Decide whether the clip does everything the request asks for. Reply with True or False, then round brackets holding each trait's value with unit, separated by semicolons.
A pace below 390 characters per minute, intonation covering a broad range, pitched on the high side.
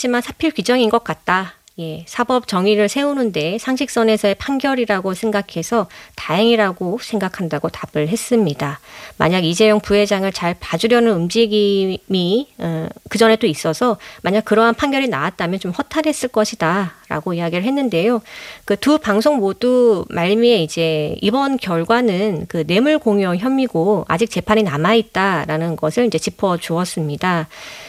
False (325 characters per minute; 5.0 semitones; 210 Hz)